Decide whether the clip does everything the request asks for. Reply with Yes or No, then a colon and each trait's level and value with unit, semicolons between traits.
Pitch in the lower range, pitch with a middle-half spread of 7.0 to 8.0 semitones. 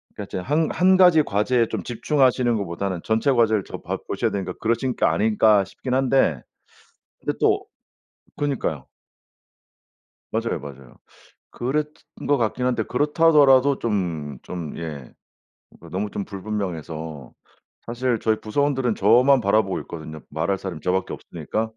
No: low, 110 Hz; wide, 6.2 semitones